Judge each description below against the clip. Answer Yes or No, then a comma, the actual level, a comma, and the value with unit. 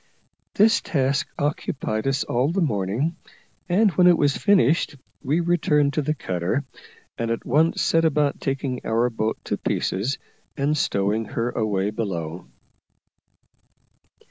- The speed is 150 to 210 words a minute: No, slow, 135 wpm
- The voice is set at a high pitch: No, low, 135 Hz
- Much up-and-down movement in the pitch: Yes, wide, 5.8 semitones